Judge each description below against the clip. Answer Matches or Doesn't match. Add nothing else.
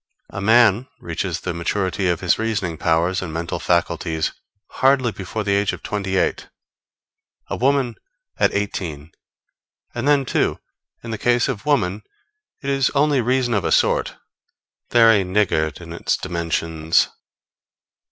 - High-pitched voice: Doesn't match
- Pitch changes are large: Matches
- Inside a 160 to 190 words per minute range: Doesn't match